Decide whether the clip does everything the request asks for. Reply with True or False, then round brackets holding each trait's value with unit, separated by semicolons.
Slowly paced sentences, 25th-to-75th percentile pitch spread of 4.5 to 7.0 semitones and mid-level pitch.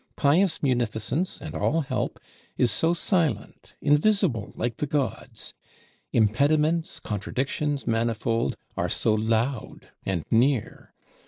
False (105 wpm; 5.1 semitones; 130 Hz)